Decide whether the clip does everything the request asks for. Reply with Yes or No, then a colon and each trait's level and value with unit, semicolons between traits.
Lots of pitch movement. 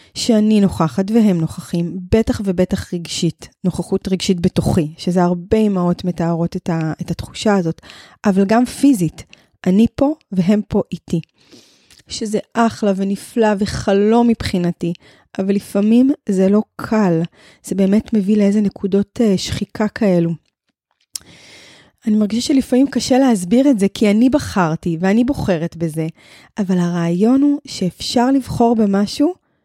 No: average, 4.0 semitones